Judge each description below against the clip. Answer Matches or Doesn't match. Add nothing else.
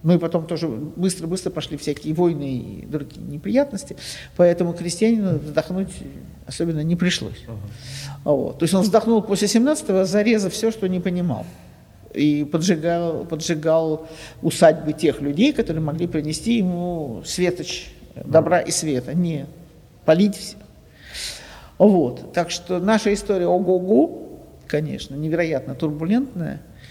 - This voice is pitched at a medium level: Matches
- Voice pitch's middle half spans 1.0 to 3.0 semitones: Doesn't match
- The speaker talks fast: Doesn't match